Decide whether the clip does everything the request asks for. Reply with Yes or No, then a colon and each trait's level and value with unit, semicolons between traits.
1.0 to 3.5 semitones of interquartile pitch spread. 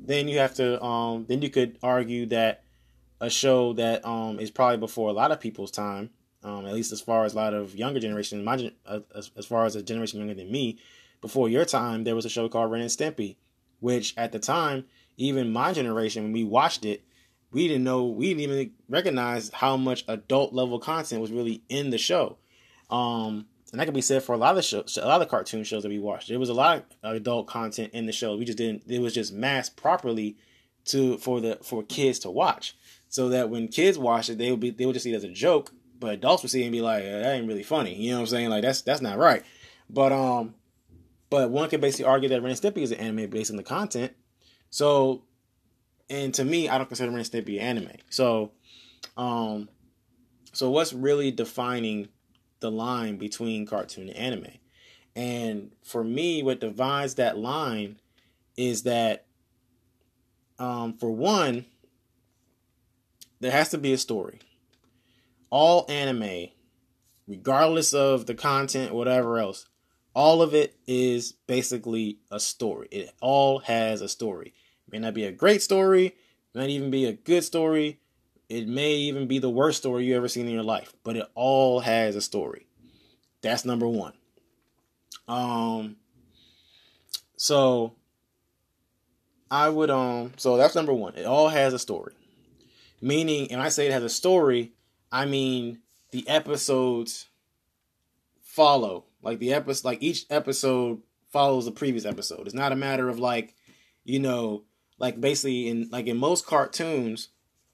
Yes: average, 2.8 semitones